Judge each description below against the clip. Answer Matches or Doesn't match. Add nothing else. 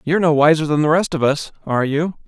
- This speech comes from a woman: Doesn't match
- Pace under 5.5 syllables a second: Doesn't match